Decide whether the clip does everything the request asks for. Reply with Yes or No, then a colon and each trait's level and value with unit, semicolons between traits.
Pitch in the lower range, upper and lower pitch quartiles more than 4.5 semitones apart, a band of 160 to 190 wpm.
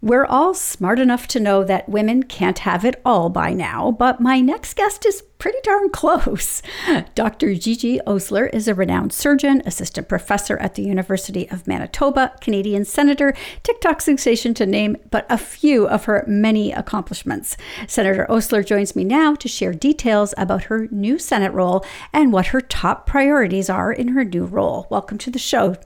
No: high, 230 Hz; wide, 5.5 semitones; average, 175 wpm